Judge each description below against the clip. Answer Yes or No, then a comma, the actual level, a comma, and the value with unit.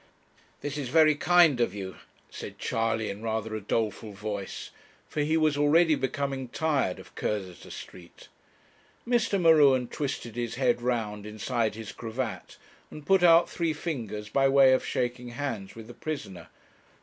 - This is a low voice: Yes, low, 125 Hz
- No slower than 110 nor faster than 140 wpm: No, average, 155 wpm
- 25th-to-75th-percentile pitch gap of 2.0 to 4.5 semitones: No, average, 5.3 semitones